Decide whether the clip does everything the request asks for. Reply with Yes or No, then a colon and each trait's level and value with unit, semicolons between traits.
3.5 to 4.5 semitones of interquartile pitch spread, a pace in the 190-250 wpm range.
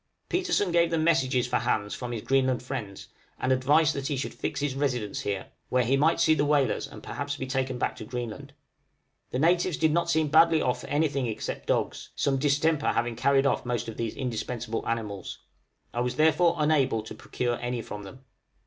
Yes: average, 3.9 semitones; fast, 205 wpm